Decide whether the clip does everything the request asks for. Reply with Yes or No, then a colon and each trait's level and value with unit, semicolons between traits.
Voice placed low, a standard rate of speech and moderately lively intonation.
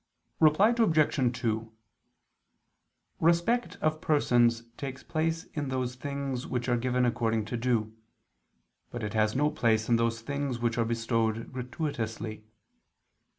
No: low, 125 Hz; slow, 130 wpm; average, 3.9 semitones